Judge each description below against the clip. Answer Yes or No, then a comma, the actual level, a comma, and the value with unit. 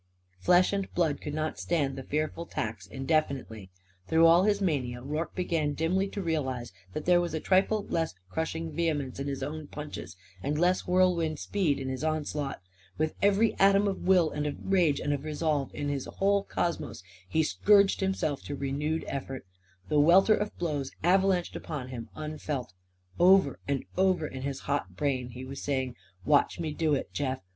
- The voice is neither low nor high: Yes, medium, 155 Hz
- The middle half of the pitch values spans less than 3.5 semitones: No, average, 4.2 semitones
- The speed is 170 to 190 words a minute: Yes, average, 180 wpm